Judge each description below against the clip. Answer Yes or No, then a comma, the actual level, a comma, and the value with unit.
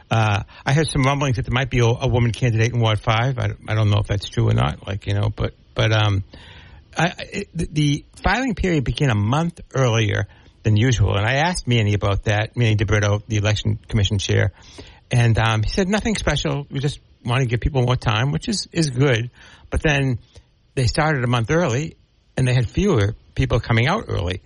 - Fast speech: Yes, fast, 215 wpm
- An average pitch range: Yes, average, 4.6 semitones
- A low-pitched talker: Yes, low, 115 Hz